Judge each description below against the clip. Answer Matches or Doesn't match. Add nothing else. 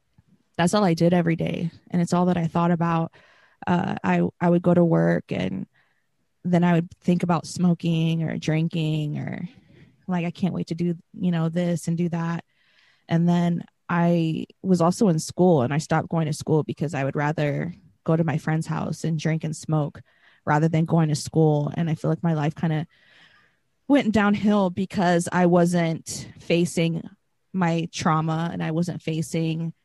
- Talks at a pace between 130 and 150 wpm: Doesn't match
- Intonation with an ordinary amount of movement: Doesn't match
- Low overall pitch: Doesn't match